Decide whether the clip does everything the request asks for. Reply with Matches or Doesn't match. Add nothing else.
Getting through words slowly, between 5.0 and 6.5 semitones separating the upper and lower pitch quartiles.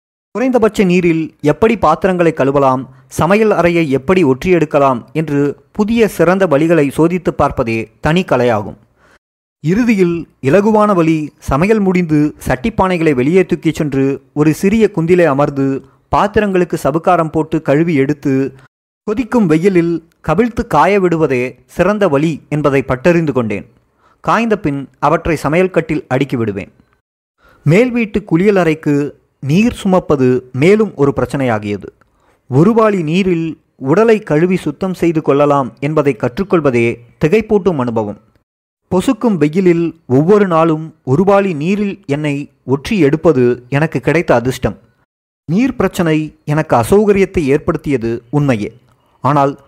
Doesn't match